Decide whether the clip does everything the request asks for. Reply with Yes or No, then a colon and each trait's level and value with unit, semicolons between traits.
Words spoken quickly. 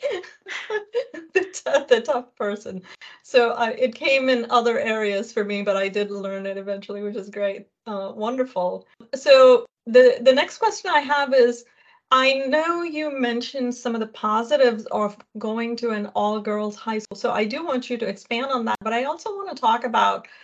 No: average, 190 wpm